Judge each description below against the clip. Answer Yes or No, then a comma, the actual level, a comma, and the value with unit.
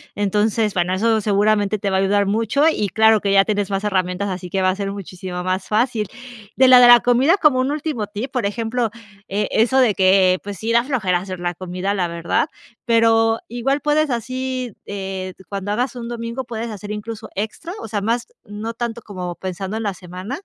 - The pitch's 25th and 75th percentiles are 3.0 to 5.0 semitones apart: Yes, average, 3.5 semitones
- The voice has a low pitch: No, high, 210 Hz